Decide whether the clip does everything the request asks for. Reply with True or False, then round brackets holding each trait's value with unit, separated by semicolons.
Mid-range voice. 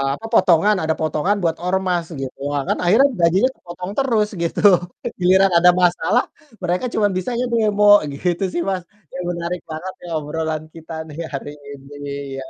True (180 Hz)